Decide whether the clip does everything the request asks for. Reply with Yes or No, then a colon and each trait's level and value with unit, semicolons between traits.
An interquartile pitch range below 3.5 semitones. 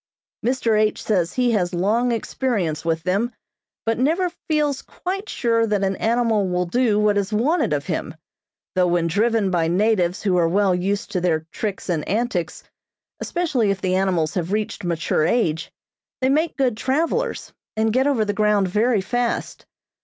No: average, 5.1 semitones